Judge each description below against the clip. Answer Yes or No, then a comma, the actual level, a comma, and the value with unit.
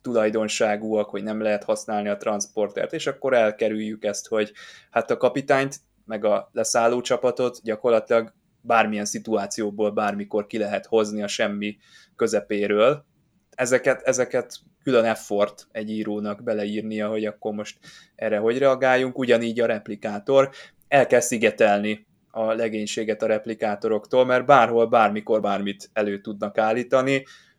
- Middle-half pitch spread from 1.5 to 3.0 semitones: Yes, narrow, 2.6 semitones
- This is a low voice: Yes, low, 110 Hz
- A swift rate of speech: No, average, 130 wpm